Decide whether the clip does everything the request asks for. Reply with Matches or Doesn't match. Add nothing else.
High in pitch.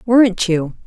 Matches